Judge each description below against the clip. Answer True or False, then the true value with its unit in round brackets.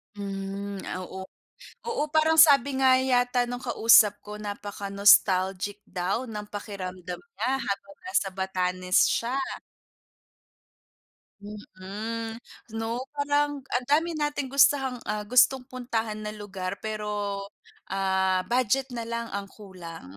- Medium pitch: False (210 Hz)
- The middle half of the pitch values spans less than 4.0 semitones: False (4.5 semitones)